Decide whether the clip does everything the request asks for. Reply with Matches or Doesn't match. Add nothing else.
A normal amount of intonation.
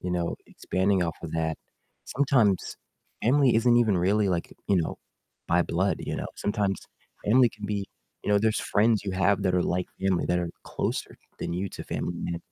Matches